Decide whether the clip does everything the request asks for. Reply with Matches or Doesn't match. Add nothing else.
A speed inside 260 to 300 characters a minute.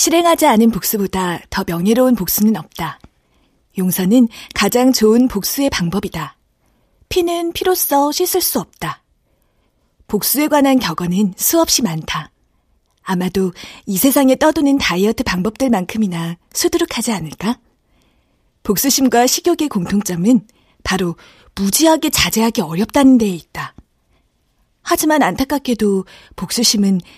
Matches